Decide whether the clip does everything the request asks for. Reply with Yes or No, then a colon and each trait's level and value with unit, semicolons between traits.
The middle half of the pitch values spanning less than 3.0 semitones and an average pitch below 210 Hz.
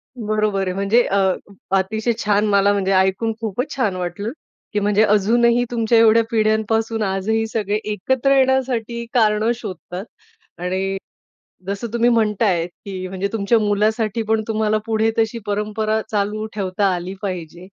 No: narrow, 2.4 semitones; high, 215 Hz